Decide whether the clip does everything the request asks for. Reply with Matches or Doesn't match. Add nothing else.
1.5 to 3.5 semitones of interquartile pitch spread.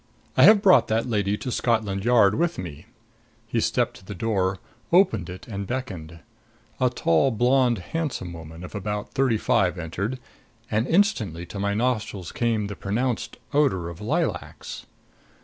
Doesn't match